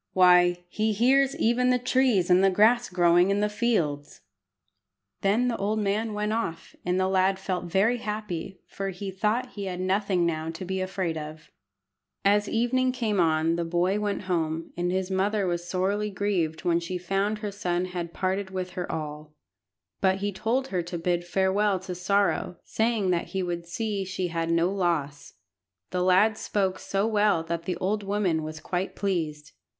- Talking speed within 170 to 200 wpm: Yes, average, 180 wpm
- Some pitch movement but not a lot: Yes, average, 3.1 semitones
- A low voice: No, high, 190 Hz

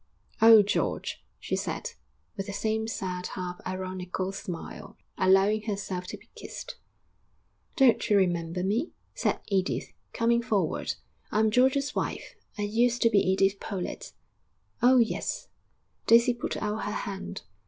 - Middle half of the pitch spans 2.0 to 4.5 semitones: Yes, average, 3.5 semitones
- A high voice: Yes, high, 205 Hz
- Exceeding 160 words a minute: No, slow, 135 wpm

